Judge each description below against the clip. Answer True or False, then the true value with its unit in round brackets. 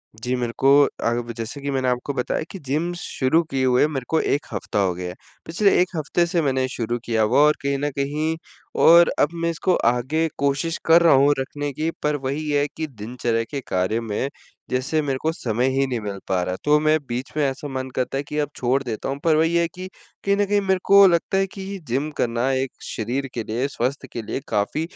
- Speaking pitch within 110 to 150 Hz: True (140 Hz)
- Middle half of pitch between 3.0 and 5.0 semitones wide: True (4.4 semitones)